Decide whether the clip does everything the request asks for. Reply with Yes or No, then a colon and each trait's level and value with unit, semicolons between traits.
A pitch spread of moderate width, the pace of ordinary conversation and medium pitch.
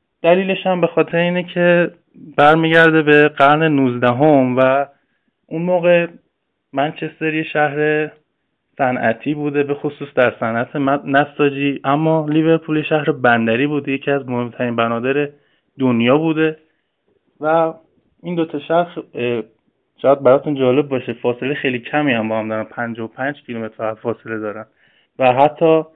Yes: average, 4.2 semitones; average, 130 wpm; medium, 145 Hz